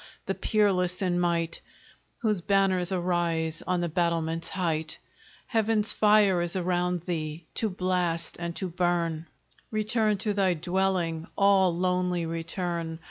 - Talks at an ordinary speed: No, slow, 130 wpm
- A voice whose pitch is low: No, medium, 180 Hz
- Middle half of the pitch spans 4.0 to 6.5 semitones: No, narrow, 2.4 semitones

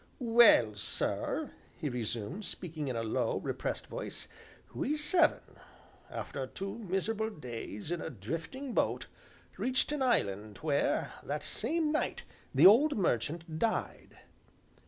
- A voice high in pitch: No, medium, 170 Hz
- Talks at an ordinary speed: No, slow, 125 wpm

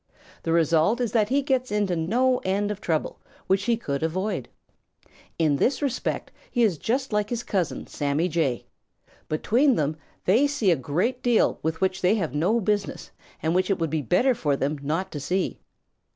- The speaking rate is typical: Yes, average, 185 wpm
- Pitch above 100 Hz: Yes, high, 190 Hz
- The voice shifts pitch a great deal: Yes, wide, 6.4 semitones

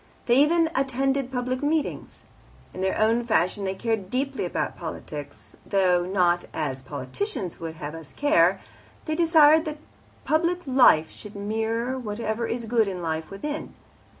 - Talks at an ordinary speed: Yes, average, 150 wpm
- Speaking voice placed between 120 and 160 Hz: No, high, 230 Hz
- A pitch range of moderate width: No, wide, 6.9 semitones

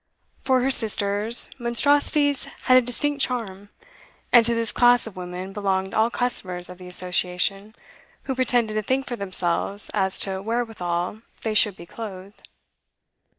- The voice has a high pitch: Yes, high, 215 Hz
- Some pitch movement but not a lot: Yes, average, 4.3 semitones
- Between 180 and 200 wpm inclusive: No, average, 150 wpm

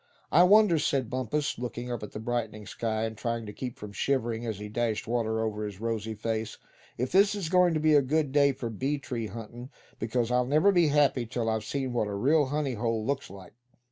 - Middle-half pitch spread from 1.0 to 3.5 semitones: No, average, 4.2 semitones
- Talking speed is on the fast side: Yes, fast, 225 wpm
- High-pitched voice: No, low, 120 Hz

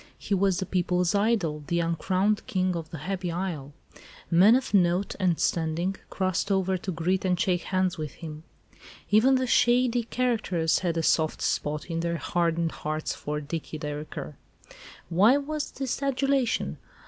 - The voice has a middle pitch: Yes, medium, 180 Hz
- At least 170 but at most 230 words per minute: No, average, 160 wpm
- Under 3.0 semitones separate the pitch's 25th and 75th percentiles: No, average, 3.8 semitones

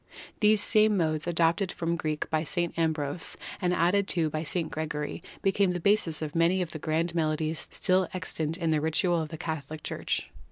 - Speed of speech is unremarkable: Yes, average, 195 wpm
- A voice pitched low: No, medium, 165 Hz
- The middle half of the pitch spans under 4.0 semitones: Yes, narrow, 2.4 semitones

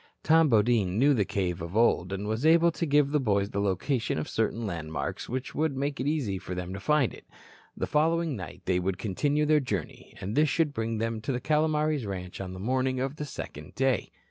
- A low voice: Yes, low, 120 Hz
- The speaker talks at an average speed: No, fast, 220 wpm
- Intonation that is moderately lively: No, wide, 7.2 semitones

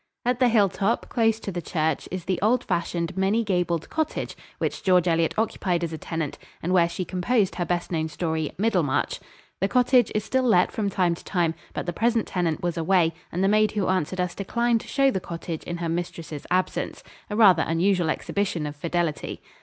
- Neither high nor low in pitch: Yes, medium, 180 Hz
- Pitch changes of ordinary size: Yes, average, 3.7 semitones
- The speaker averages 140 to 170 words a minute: No, average, 200 wpm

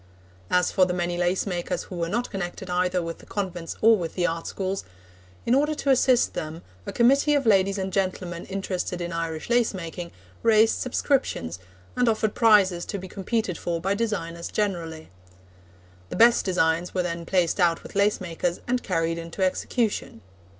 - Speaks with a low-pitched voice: No, medium, 185 Hz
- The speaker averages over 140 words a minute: Yes, average, 180 wpm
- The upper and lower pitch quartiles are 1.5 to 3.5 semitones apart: No, average, 3.9 semitones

